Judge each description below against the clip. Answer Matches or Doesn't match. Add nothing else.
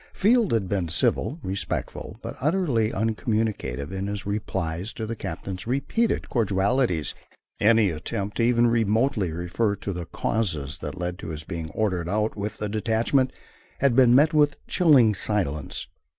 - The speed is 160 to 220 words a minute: Doesn't match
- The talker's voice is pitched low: Matches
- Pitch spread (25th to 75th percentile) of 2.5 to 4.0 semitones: Doesn't match